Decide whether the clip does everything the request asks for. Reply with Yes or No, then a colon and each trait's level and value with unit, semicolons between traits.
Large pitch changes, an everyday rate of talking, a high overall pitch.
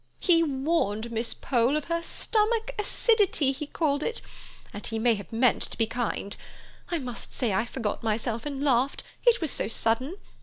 Yes: wide, 6.5 semitones; average, 175 wpm; very high, 265 Hz